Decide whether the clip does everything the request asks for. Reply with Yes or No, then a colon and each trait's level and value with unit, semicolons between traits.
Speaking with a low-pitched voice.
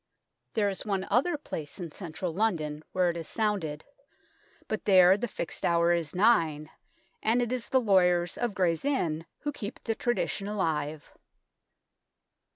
No: medium, 185 Hz